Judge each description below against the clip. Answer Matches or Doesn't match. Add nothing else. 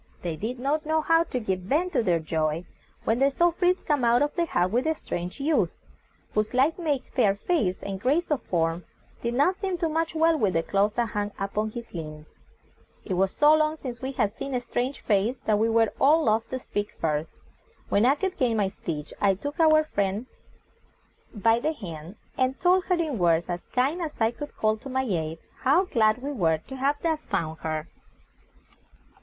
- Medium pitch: Doesn't match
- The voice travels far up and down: Matches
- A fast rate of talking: Matches